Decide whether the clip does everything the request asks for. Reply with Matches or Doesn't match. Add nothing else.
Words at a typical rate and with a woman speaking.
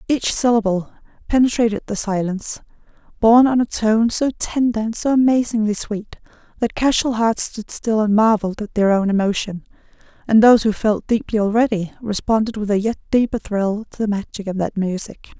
Matches